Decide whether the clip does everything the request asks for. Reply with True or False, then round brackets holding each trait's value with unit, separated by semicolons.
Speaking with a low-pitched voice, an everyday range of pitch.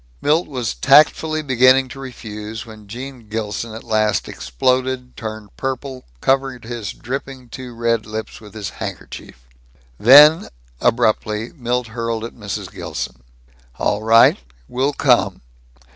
True (120 Hz; 3.3 semitones)